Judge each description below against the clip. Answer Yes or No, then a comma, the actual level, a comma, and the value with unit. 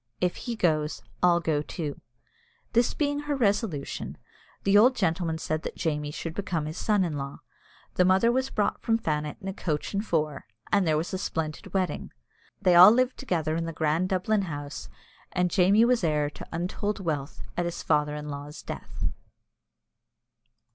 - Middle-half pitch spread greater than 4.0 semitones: Yes, average, 4.9 semitones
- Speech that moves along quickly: No, average, 175 wpm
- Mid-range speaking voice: Yes, medium, 175 Hz